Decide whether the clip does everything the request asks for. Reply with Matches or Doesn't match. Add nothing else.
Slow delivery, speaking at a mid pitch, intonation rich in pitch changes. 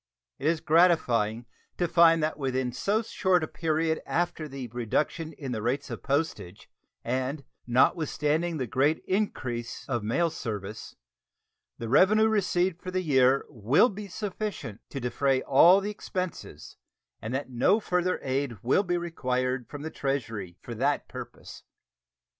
Doesn't match